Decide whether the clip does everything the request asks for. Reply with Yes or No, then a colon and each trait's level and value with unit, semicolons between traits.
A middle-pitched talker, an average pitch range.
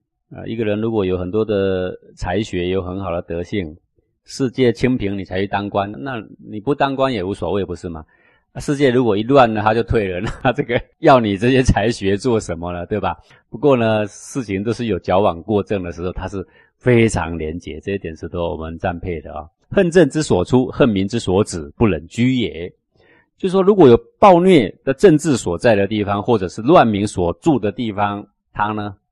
No: low, 105 Hz; average, 5.0 semitones